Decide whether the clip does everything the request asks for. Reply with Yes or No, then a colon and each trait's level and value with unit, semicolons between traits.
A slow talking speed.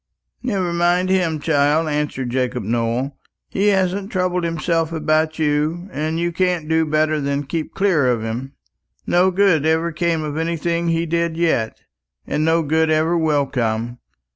No: average, 160 wpm